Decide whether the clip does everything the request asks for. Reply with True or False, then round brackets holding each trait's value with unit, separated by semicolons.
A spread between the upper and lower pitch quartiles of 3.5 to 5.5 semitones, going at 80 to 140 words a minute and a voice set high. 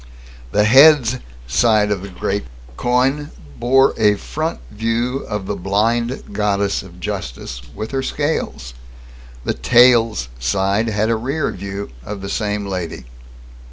False (3.9 semitones; 135 wpm; 105 Hz)